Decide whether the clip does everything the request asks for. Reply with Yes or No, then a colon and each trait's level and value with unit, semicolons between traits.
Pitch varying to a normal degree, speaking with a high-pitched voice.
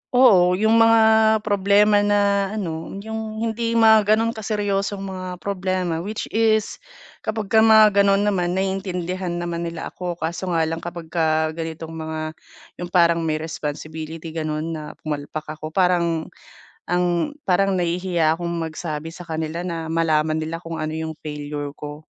No: average, 3.8 semitones; medium, 175 Hz